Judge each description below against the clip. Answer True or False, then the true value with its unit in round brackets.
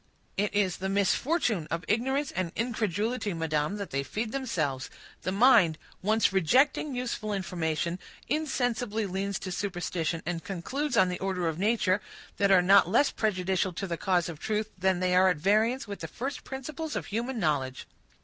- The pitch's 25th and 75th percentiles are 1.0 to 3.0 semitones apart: False (4.6 semitones)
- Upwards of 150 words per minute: True (170 wpm)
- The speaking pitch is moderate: False (195 Hz)